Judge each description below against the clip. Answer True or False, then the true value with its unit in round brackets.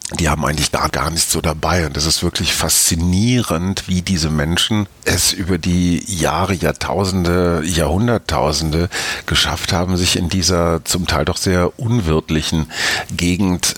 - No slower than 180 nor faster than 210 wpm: False (150 wpm)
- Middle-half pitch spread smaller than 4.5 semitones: True (2.4 semitones)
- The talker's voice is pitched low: True (85 Hz)